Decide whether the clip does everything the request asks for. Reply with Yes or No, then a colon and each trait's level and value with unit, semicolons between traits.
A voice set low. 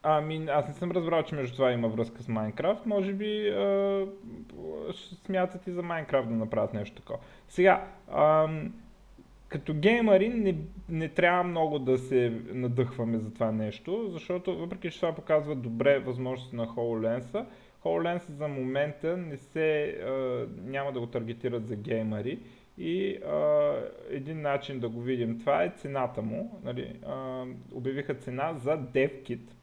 No: medium, 150 Hz